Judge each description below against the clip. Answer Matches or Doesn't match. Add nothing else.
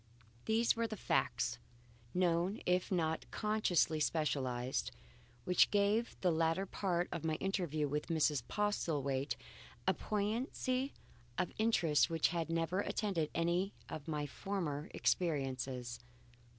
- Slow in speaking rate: Matches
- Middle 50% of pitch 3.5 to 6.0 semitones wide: Matches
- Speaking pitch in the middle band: Matches